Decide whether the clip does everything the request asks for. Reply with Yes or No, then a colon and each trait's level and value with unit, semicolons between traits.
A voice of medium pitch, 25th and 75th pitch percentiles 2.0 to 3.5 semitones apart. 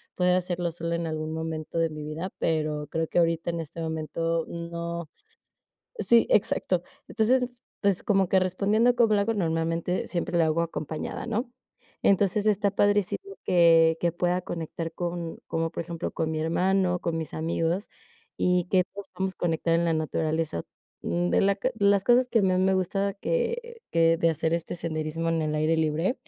Yes: medium, 170 Hz; average, 3.0 semitones